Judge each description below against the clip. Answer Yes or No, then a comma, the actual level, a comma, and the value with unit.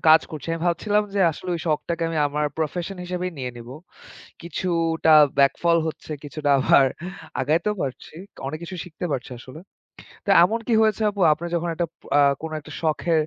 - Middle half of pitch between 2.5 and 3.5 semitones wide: Yes, average, 2.8 semitones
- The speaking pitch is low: No, medium, 165 Hz